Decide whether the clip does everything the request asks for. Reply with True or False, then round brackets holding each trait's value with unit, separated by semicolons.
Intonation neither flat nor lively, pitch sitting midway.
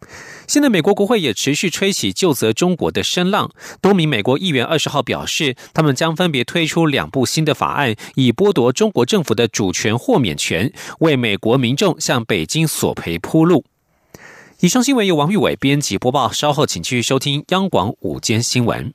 False (6.7 semitones; 150 Hz)